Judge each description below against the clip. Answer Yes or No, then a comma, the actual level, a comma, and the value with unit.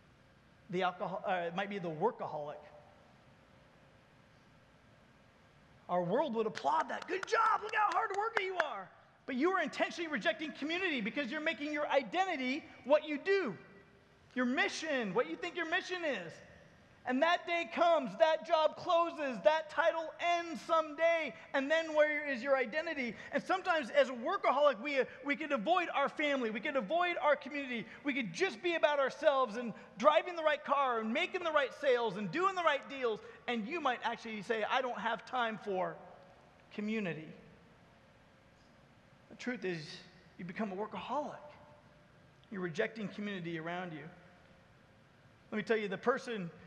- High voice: Yes, very high, 275 Hz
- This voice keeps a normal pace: Yes, average, 160 wpm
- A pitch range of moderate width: No, wide, 6.7 semitones